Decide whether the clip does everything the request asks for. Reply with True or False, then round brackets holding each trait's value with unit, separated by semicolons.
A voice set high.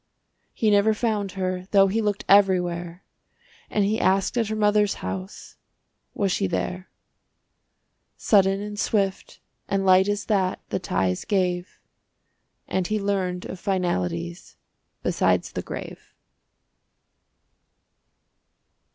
True (195 Hz)